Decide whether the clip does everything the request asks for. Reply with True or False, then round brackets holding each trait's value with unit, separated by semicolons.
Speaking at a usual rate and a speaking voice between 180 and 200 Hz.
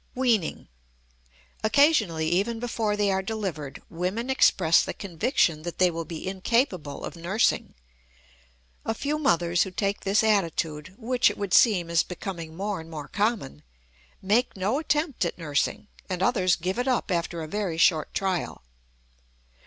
True (155 wpm; 190 Hz)